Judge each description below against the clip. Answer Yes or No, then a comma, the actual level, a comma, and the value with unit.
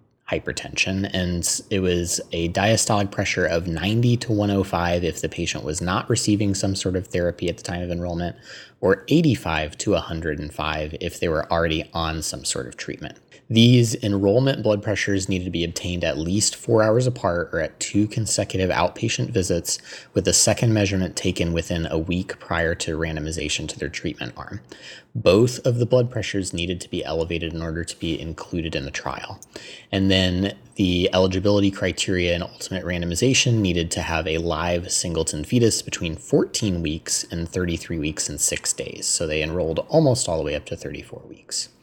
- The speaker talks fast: No, average, 180 wpm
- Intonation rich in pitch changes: No, average, 3.6 semitones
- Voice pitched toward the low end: Yes, very low, 90 Hz